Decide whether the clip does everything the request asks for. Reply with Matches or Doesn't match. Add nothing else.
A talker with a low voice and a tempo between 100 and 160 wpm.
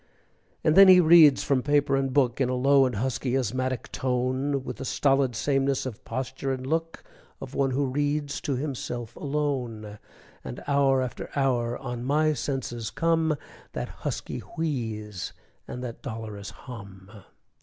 Matches